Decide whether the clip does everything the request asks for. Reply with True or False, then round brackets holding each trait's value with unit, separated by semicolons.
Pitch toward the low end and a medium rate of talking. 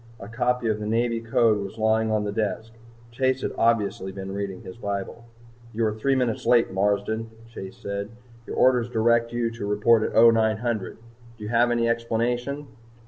True (115 Hz; 180 wpm)